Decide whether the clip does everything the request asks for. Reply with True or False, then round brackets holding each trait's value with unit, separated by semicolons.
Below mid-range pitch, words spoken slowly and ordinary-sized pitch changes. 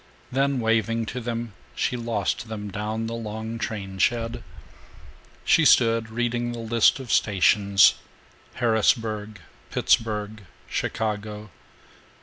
False (110 Hz; 110 wpm; 1.7 semitones)